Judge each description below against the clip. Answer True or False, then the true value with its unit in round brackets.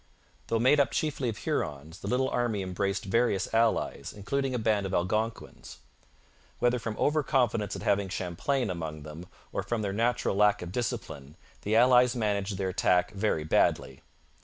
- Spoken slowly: False (165 wpm)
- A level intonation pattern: False (4.5 semitones)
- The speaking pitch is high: False (105 Hz)